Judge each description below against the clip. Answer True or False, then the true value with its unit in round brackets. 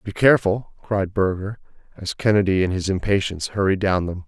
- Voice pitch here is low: True (95 Hz)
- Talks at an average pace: True (170 wpm)